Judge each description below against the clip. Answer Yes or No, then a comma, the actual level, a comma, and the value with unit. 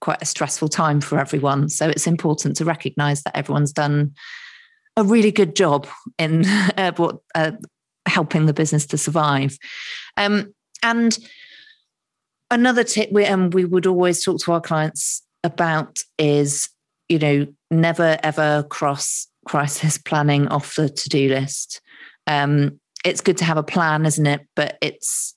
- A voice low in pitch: No, medium, 155 Hz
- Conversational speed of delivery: Yes, average, 155 wpm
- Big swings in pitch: No, average, 3.9 semitones